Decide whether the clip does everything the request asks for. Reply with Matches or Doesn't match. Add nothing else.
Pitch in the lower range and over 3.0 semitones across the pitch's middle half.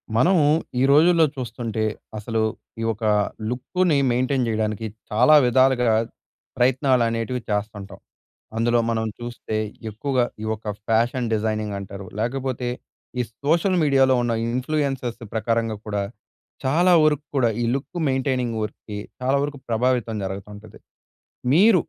Matches